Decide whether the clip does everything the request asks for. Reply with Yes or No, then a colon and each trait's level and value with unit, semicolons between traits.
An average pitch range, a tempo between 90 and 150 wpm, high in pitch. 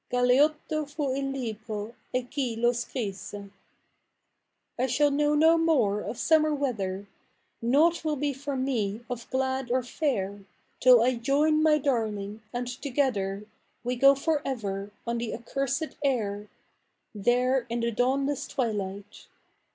Yes: average, 4.1 semitones; slow, 135 wpm; very high, 250 Hz